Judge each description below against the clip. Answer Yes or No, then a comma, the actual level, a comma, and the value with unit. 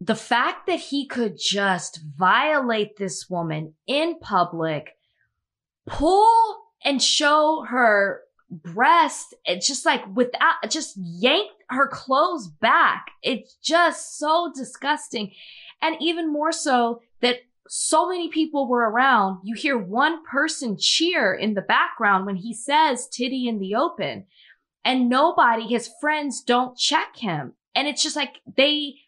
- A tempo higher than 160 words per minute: No, slow, 135 wpm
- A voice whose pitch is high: Yes, very high, 260 Hz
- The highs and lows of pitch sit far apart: Yes, wide, 5.7 semitones